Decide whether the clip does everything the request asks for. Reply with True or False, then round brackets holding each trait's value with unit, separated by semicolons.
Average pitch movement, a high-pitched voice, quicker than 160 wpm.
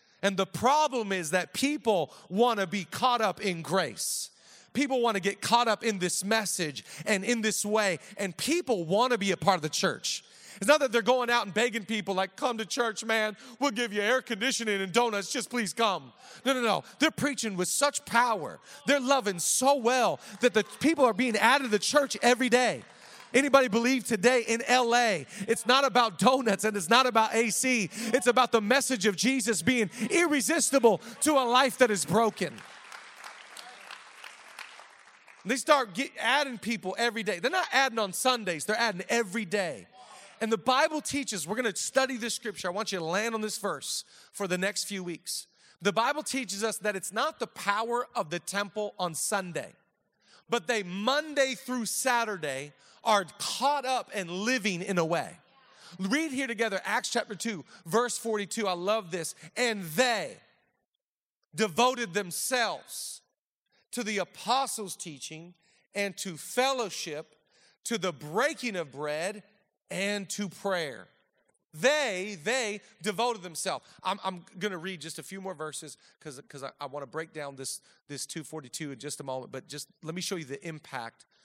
True (4.7 semitones; 215 Hz; 180 wpm)